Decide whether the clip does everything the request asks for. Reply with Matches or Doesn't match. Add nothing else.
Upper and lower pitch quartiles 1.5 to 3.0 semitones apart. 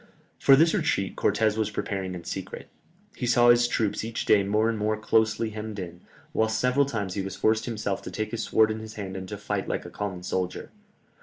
Matches